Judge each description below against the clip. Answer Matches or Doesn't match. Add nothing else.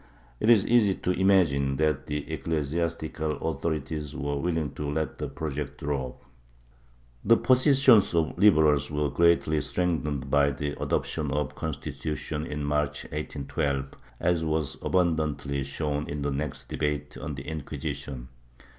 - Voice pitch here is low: Matches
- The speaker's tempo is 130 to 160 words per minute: Matches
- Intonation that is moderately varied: Doesn't match